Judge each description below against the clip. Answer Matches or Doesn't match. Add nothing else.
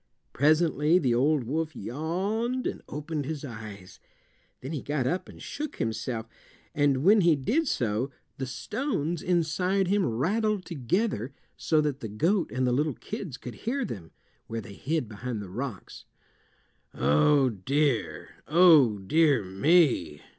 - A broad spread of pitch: Matches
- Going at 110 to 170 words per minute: Matches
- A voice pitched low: Doesn't match